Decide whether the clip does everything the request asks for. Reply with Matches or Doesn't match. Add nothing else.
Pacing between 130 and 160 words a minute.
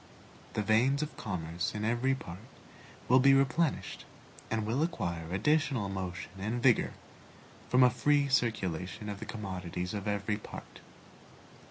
Matches